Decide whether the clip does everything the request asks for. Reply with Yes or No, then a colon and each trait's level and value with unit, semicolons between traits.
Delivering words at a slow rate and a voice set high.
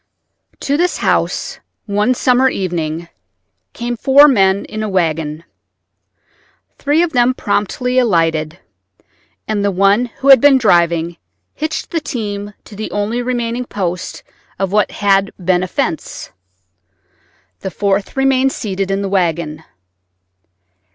Yes: slow, 130 wpm; high, 205 Hz